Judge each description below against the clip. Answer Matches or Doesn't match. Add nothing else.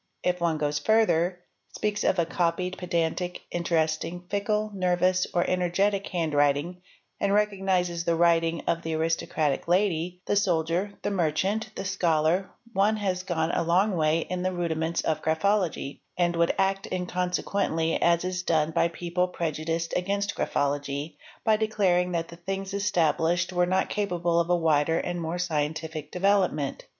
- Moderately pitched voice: Matches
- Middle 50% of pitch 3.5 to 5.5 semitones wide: Doesn't match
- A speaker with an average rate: Matches